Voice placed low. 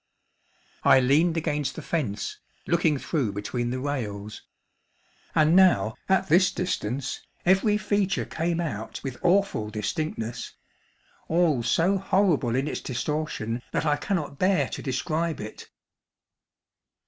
No: medium, 150 Hz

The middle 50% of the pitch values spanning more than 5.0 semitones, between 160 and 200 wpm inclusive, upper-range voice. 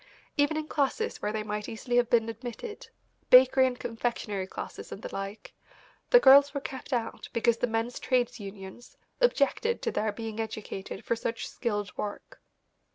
No: average, 3.6 semitones; average, 165 wpm; high, 235 Hz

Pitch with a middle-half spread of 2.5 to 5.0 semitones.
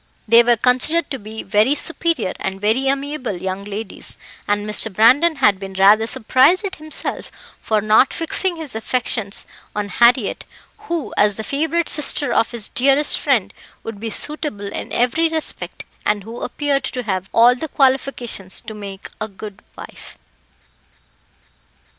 No: wide, 5.4 semitones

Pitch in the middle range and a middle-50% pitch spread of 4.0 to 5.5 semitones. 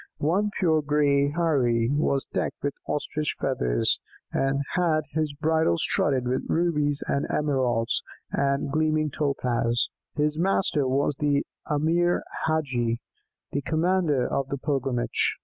No: medium, 145 Hz; average, 2.7 semitones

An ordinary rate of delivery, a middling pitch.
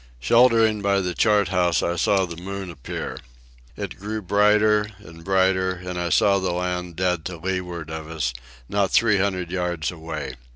No: average, 170 wpm; very low, 90 Hz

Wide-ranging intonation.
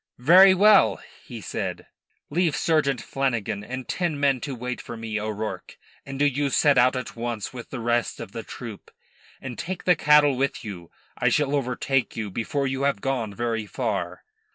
No: average, 3.8 semitones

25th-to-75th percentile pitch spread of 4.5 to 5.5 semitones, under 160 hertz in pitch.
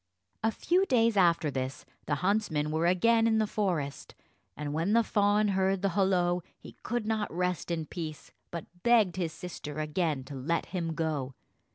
No: average, 5.1 semitones; medium, 180 Hz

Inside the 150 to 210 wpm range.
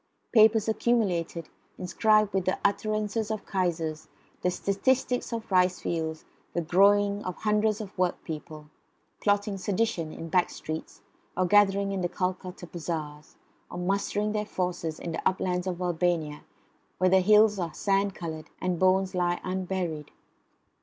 No: average, 140 wpm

